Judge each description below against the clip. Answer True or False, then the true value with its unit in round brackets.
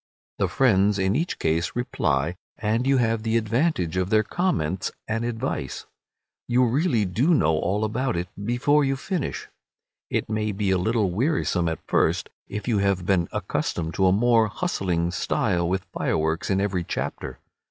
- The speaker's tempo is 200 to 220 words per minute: False (165 wpm)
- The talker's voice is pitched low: True (105 Hz)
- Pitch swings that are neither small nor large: True (5.0 semitones)